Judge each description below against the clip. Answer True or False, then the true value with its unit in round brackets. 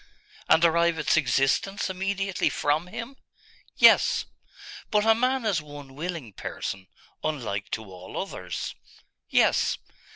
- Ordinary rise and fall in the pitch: False (6.6 semitones)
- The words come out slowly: True (120 wpm)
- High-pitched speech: False (160 Hz)